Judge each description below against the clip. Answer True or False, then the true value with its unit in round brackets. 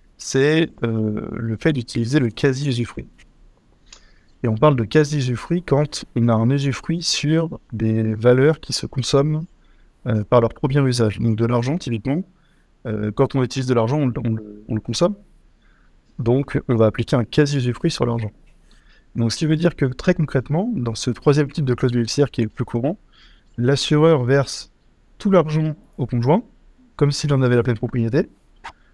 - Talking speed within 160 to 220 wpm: True (175 wpm)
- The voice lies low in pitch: True (130 Hz)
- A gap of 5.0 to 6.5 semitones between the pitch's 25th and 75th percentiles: False (4.6 semitones)